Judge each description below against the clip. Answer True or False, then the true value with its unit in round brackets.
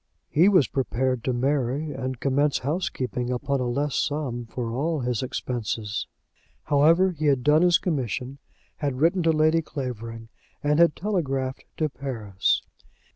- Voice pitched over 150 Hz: False (135 Hz)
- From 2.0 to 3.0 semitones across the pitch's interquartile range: False (3.7 semitones)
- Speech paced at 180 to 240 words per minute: False (145 wpm)